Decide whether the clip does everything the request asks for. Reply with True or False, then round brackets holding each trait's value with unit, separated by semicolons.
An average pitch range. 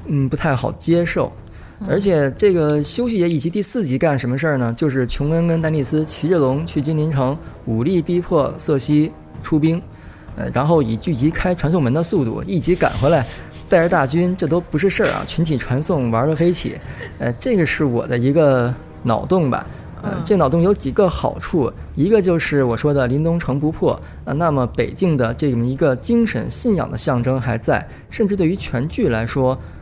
True (4.7 semitones)